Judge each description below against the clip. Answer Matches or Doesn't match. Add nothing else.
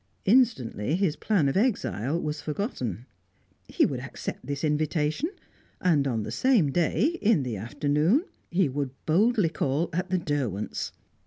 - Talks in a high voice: Doesn't match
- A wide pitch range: Matches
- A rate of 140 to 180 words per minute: Matches